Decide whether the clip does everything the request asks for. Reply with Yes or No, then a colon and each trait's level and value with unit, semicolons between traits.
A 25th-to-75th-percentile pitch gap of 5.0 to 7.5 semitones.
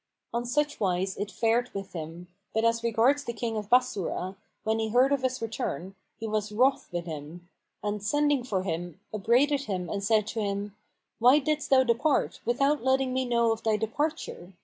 No: average, 4.6 semitones